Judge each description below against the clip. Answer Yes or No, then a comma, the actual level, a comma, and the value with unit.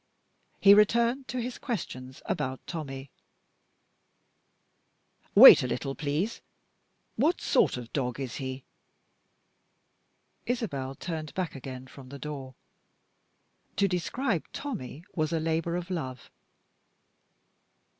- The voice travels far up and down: Yes, wide, 7.0 semitones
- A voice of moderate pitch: Yes, medium, 155 Hz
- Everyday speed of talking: No, slow, 105 wpm